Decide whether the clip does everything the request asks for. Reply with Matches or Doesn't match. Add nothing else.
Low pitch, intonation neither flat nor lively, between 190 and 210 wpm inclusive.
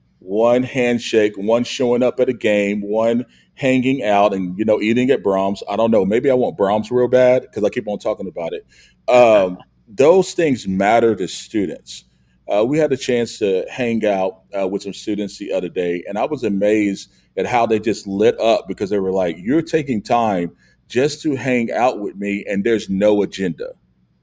Matches